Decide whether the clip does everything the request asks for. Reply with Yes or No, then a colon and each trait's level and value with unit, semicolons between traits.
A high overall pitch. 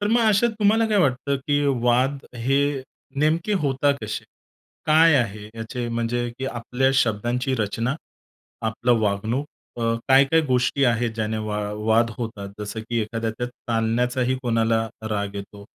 No: low, 120 Hz